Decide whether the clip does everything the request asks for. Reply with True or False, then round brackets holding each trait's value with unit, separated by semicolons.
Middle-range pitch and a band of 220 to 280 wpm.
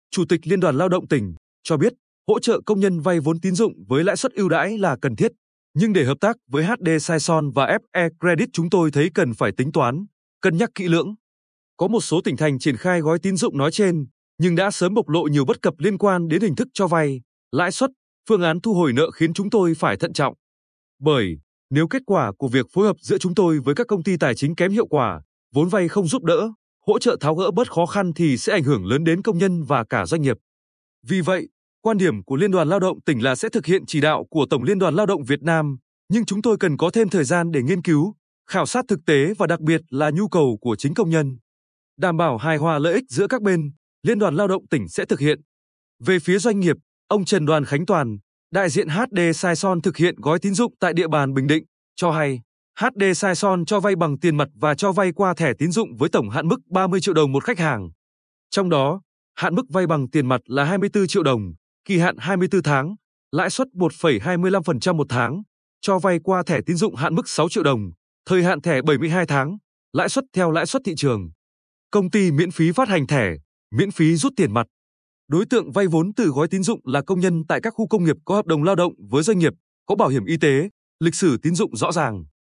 True (170 Hz; 245 wpm)